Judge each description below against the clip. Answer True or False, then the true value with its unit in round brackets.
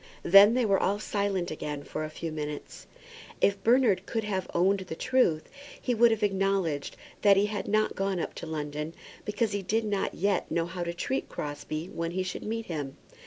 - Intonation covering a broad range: False (4.1 semitones)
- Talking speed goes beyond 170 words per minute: True (200 wpm)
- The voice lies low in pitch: False (195 Hz)